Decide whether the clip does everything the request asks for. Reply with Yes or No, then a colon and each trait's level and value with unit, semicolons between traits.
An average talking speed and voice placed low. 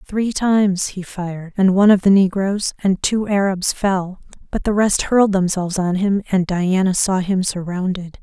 No: average, 180 wpm; high, 190 Hz